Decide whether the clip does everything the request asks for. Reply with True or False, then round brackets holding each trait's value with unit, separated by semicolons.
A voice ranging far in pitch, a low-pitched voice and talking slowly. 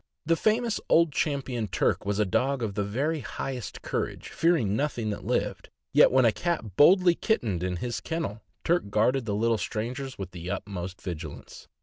False (6.8 semitones; 115 Hz; 180 wpm)